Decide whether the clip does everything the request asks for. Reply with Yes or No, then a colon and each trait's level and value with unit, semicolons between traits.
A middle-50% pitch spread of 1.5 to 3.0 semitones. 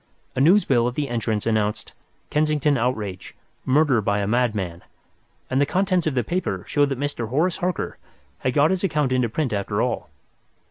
No: average, 5.3 semitones